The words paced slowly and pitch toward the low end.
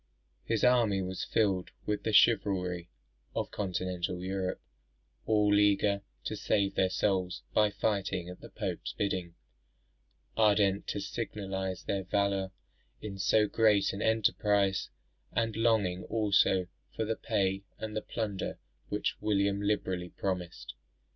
Yes: slow, 130 wpm; low, 100 Hz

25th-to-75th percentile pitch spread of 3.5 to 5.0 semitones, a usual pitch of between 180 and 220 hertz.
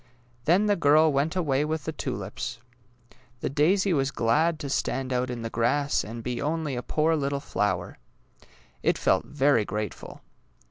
No: average, 4.3 semitones; medium, 140 Hz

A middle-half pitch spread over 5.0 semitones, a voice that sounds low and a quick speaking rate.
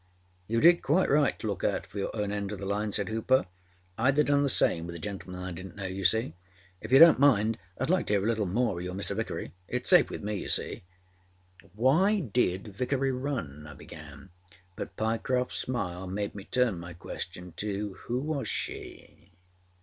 Yes: wide, 5.6 semitones; low, 105 Hz; fast, 210 wpm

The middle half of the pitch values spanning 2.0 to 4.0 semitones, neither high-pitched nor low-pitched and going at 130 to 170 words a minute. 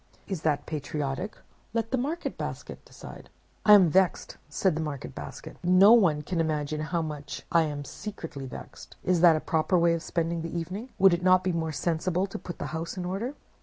No: average, 3.3 semitones; medium, 170 Hz; fast, 205 wpm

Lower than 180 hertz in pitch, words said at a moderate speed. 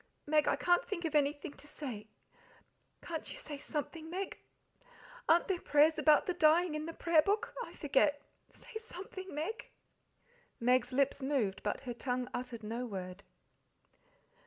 No: very high, 295 Hz; average, 160 wpm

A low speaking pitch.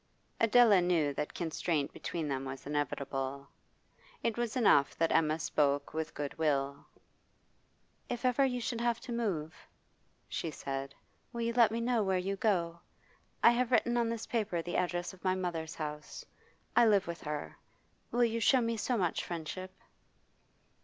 No: medium, 180 Hz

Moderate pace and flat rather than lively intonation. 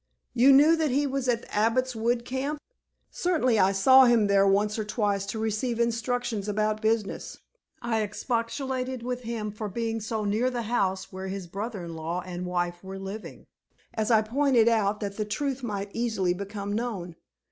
No: average, 180 wpm; average, 3.5 semitones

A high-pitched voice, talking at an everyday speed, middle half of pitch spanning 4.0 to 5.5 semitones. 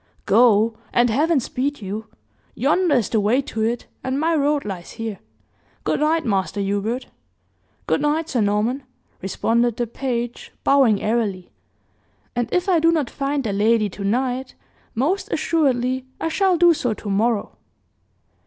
Yes: high, 245 Hz; average, 155 wpm; average, 5.0 semitones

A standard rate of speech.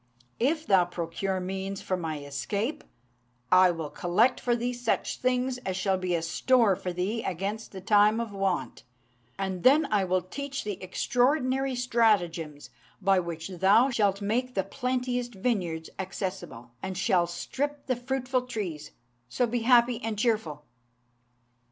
Yes: average, 150 wpm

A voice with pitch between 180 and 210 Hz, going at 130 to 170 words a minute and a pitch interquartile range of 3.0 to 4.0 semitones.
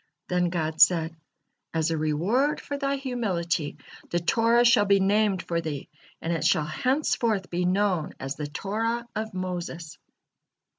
No: medium, 185 Hz; average, 150 wpm; wide, 5.6 semitones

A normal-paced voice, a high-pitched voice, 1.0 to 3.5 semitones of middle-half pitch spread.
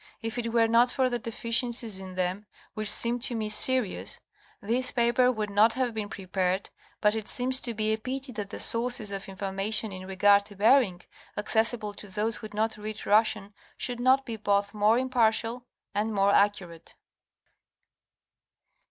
Yes: average, 170 wpm; high, 220 Hz; average, 2.8 semitones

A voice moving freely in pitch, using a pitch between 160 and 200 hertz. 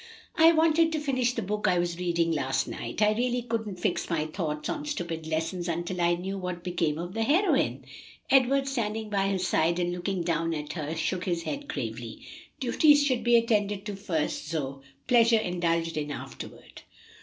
Yes: wide, 6.0 semitones; medium, 185 Hz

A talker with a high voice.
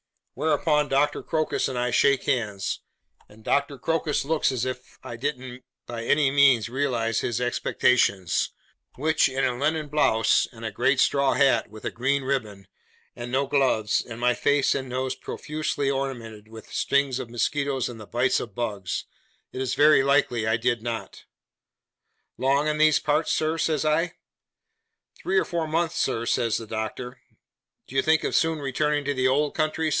No: low, 130 Hz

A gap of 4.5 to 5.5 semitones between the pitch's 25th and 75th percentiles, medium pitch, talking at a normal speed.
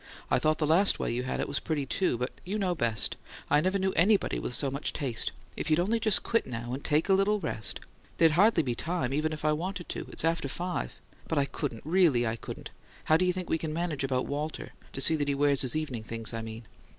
No: average, 5.2 semitones; medium, 155 Hz; fast, 255 wpm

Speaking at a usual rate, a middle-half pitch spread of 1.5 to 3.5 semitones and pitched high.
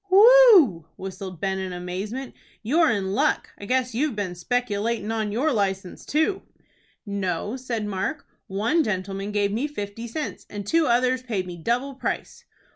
No: average, 155 wpm; average, 5.1 semitones; high, 215 Hz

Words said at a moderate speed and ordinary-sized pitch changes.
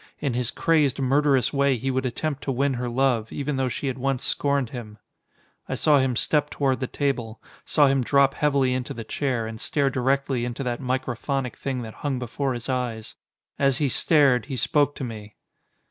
No: average, 195 wpm; narrow, 2.2 semitones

